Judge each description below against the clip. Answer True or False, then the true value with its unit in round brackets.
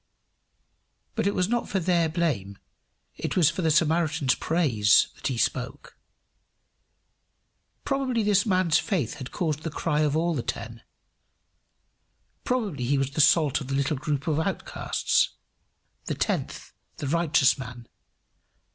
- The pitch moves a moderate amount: True (4.2 semitones)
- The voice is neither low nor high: True (155 Hz)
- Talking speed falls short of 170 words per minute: True (140 wpm)